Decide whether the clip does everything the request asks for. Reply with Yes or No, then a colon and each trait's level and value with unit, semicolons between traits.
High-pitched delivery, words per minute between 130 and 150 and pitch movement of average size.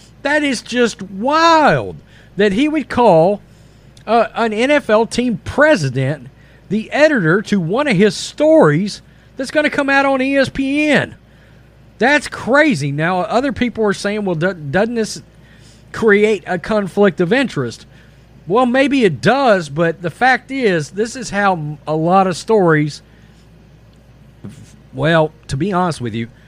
No: high, 210 Hz; average, 145 wpm; wide, 7.6 semitones